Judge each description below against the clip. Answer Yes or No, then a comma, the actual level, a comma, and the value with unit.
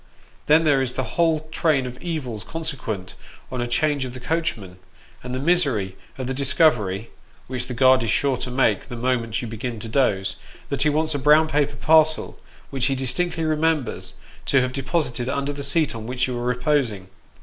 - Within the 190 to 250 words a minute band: Yes, average, 195 wpm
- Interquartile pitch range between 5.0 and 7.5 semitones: No, average, 3.9 semitones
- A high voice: No, low, 130 Hz